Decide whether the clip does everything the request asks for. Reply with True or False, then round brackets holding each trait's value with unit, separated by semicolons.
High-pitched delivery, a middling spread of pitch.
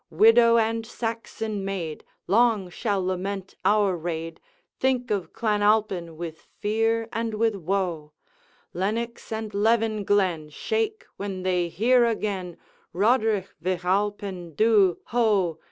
True (205 Hz; 3.6 semitones)